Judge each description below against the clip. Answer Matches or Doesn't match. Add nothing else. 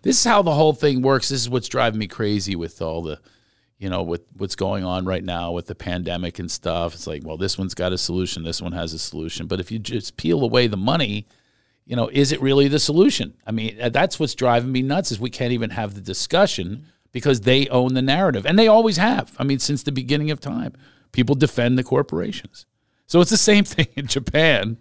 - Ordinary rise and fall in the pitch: Doesn't match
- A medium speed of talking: Doesn't match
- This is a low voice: Matches